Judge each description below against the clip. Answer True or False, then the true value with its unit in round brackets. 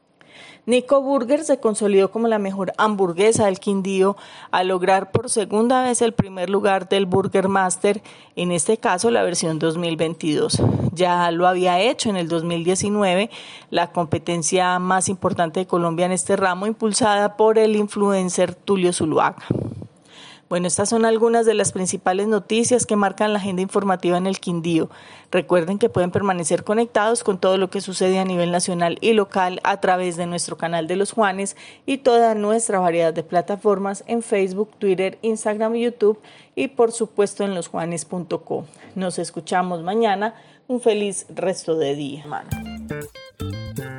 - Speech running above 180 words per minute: False (155 wpm)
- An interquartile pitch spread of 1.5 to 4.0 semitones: True (3.4 semitones)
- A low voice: False (190 Hz)